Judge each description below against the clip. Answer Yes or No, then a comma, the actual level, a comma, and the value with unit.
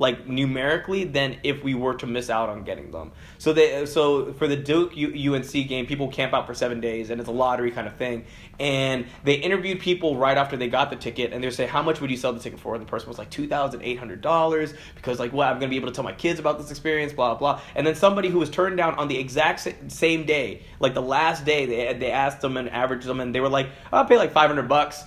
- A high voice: No, medium, 140 Hz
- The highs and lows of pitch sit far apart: No, average, 3.3 semitones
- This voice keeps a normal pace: No, fast, 260 wpm